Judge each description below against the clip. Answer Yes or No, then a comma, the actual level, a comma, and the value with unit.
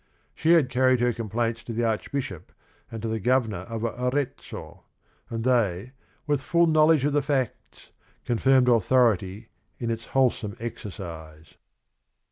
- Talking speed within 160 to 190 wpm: No, average, 140 wpm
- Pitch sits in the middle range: No, low, 120 Hz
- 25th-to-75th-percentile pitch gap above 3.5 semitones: No, average, 3.1 semitones